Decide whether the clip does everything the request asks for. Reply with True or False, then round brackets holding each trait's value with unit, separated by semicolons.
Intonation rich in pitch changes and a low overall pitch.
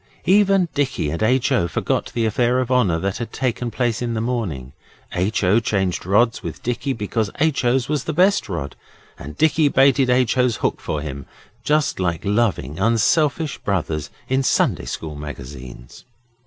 True (7.0 semitones; 115 Hz)